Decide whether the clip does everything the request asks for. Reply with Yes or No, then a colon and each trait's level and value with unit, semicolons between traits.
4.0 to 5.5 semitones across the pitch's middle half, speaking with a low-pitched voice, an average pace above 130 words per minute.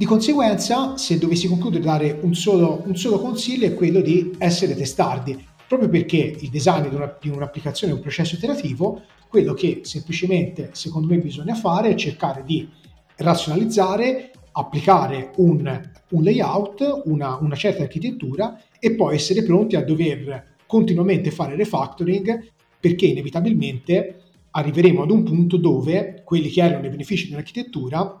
No: average, 4.7 semitones; medium, 175 Hz; average, 145 wpm